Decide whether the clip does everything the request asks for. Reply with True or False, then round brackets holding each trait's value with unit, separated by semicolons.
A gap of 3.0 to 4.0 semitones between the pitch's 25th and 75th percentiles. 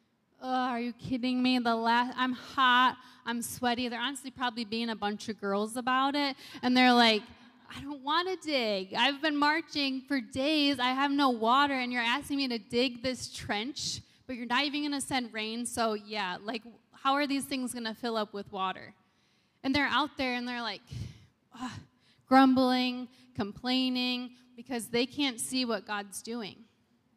False (2.5 semitones)